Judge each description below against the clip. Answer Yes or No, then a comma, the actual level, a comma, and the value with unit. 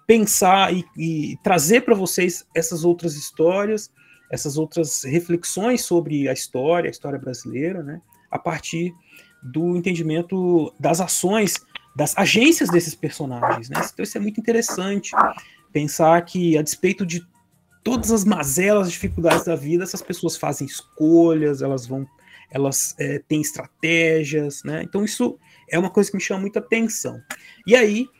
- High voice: No, medium, 170 Hz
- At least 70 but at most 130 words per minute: No, average, 150 wpm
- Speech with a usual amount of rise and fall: Yes, average, 4.1 semitones